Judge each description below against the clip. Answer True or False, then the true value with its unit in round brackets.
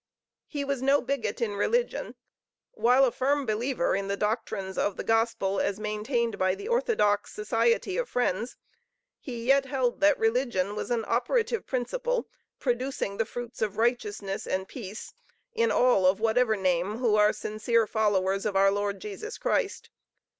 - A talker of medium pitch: False (230 Hz)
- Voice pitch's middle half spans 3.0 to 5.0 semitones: True (4.2 semitones)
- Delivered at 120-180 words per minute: True (160 wpm)